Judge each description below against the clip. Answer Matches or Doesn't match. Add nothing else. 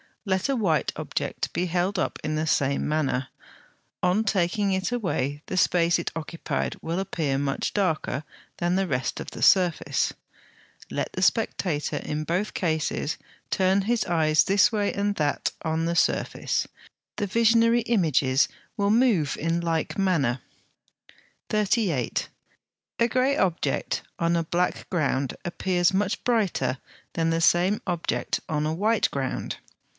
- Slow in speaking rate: Doesn't match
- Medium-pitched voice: Matches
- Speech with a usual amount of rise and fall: Matches